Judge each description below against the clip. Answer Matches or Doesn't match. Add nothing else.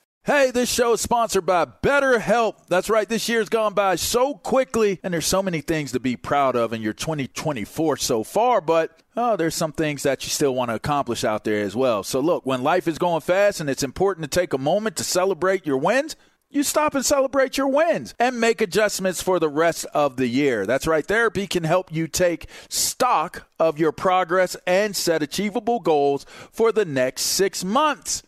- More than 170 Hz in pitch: Matches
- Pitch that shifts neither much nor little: Doesn't match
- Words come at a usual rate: Doesn't match